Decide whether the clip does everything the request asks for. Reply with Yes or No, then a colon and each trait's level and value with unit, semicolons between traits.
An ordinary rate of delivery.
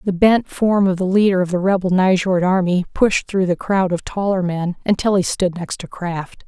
No: fast, 220 wpm